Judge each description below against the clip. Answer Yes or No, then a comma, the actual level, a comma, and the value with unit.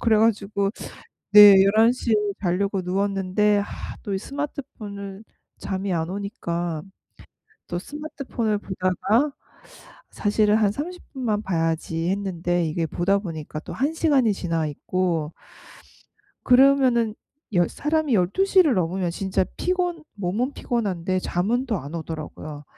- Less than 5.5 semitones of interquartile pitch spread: Yes, average, 5.1 semitones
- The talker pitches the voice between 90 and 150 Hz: No, high, 200 Hz